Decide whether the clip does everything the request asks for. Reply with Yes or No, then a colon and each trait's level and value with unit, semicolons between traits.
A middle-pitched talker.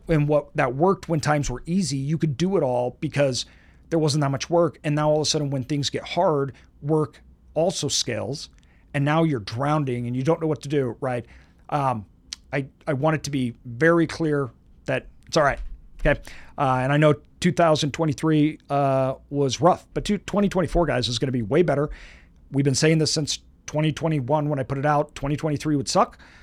Yes: medium, 145 Hz